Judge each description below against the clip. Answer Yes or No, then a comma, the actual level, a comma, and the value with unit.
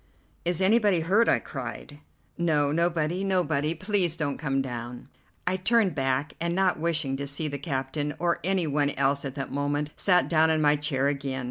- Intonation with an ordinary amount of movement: Yes, average, 3.8 semitones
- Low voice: No, medium, 150 Hz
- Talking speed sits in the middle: Yes, average, 185 wpm